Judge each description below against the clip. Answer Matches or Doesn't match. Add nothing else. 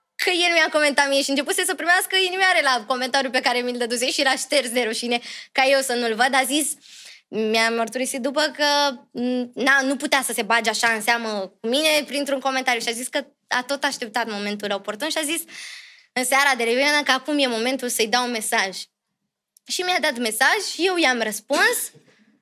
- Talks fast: Matches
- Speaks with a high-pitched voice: Matches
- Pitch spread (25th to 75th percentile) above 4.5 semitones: Doesn't match